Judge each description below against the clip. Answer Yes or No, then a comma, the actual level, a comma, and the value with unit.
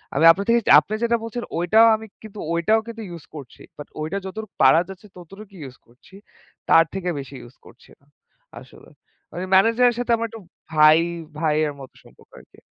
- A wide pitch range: Yes, wide, 6.1 semitones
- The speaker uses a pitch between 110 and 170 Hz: No, high, 190 Hz